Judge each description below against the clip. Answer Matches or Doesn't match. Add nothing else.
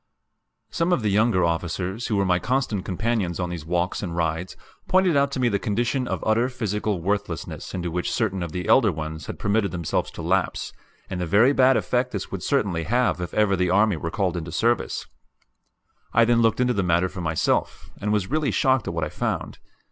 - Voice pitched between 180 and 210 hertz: Doesn't match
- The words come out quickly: Matches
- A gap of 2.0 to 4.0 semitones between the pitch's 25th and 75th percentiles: Doesn't match